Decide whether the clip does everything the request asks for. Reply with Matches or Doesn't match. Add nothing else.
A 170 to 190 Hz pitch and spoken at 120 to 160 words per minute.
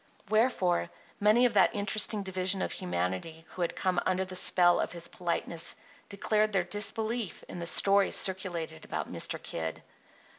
Matches